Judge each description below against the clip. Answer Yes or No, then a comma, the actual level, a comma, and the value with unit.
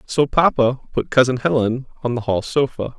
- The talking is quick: No, average, 180 wpm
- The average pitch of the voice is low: Yes, low, 130 Hz